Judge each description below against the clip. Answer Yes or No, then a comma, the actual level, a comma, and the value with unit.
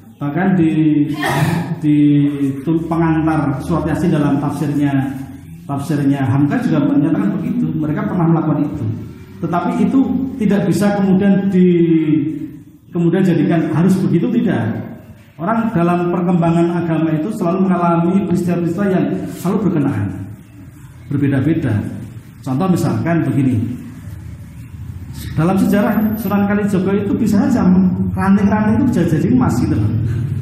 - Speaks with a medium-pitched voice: Yes, medium, 160 Hz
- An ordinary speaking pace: Yes, average, 110 wpm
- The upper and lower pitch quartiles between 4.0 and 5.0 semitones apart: Yes, average, 4.6 semitones